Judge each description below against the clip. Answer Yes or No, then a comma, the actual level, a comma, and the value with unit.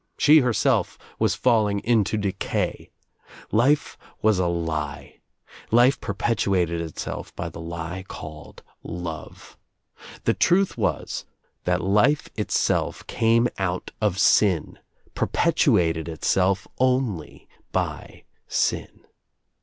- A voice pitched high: No, very low, 95 Hz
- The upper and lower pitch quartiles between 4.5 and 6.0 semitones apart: Yes, wide, 5.6 semitones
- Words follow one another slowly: Yes, slow, 105 wpm